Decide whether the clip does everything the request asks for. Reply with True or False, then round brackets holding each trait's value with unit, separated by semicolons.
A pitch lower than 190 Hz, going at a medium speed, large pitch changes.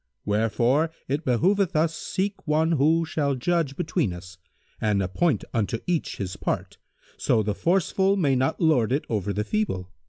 True (140 Hz; 165 wpm; 7.6 semitones)